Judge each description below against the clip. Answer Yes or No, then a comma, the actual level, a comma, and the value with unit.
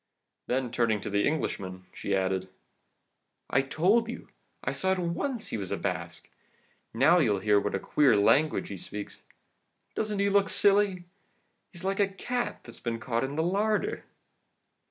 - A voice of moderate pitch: Yes, medium, 155 Hz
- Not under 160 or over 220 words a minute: Yes, average, 170 wpm